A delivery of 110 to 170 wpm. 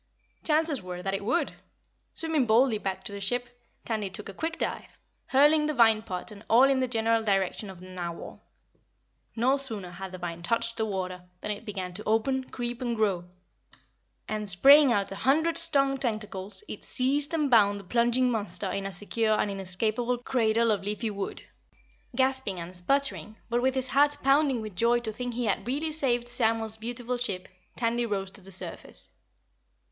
No: average, 185 wpm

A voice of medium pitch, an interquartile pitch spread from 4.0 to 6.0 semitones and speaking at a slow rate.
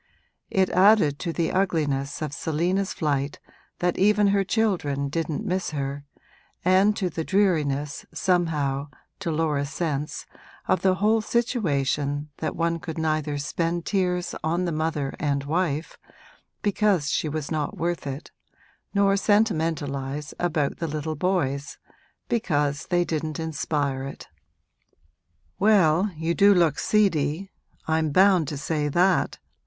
Yes: medium, 160 Hz; average, 4.3 semitones; slow, 130 wpm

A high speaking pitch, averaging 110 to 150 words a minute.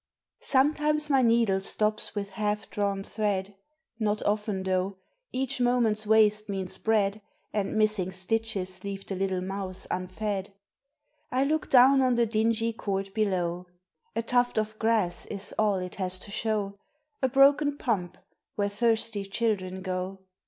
Yes: high, 210 Hz; average, 145 wpm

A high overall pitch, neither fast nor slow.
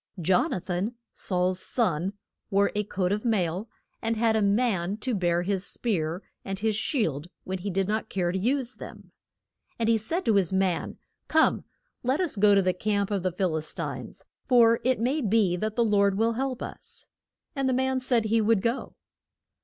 Yes: high, 210 Hz; average, 195 wpm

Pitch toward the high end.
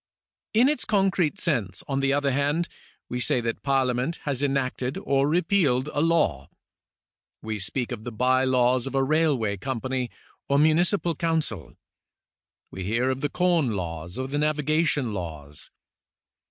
No: low, 135 Hz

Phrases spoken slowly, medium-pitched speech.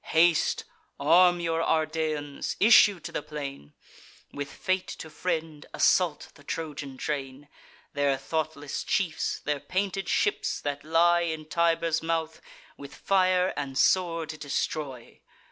Yes: slow, 125 wpm; medium, 160 Hz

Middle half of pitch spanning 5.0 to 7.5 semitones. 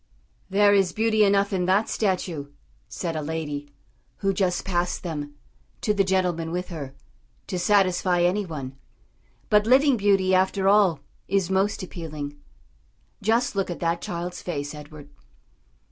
No: average, 3.4 semitones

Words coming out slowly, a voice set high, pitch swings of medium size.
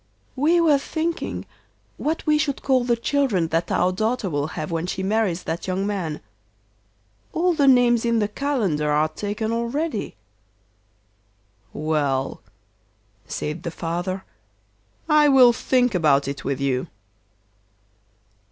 No: slow, 130 wpm; high, 205 Hz; wide, 8.5 semitones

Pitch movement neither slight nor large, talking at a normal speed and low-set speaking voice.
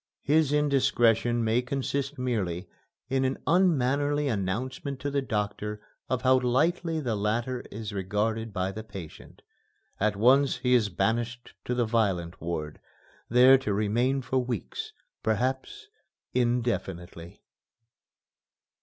No: average, 4.0 semitones; slow, 120 wpm; low, 120 Hz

